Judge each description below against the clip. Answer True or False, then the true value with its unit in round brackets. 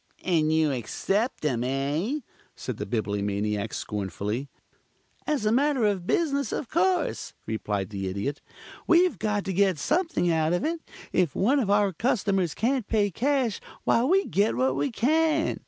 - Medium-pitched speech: False (195 Hz)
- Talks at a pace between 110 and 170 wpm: True (155 wpm)